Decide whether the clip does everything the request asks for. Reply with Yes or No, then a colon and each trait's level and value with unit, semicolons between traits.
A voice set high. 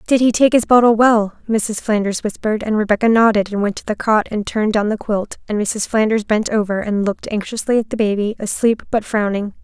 Yes: high, 215 Hz